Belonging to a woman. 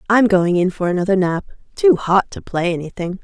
Yes: female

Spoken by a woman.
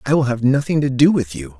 No: male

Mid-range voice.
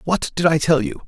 Yes: medium, 165 Hz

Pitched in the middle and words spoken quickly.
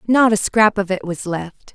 No: high, 200 Hz; fast, 240 wpm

